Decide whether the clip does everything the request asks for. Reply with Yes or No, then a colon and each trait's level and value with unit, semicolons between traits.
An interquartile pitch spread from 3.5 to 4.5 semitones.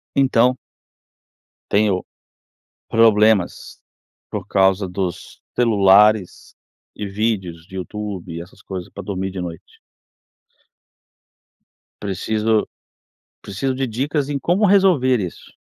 Yes: average, 4.1 semitones